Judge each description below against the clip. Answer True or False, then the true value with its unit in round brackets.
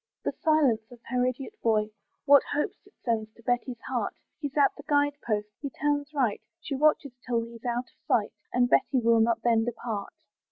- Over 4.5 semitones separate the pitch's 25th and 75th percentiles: False (3.8 semitones)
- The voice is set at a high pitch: True (245 Hz)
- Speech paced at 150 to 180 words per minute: False (195 wpm)